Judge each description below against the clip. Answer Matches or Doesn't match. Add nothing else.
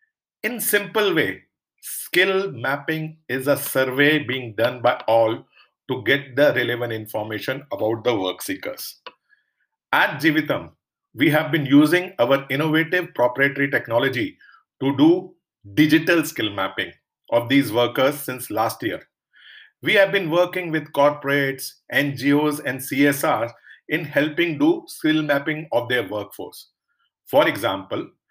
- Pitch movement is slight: Doesn't match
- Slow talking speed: Matches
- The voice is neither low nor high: Matches